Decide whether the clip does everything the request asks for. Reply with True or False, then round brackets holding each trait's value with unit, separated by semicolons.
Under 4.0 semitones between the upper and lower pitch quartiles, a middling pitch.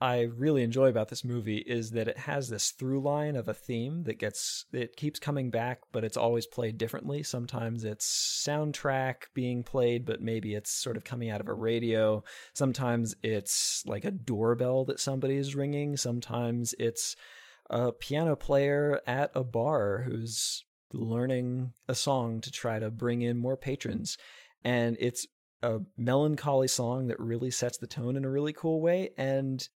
False (2.8 semitones; 125 Hz)